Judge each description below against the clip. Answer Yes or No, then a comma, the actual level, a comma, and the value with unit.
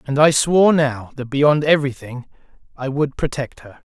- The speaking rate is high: No, average, 170 wpm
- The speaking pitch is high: No, medium, 140 Hz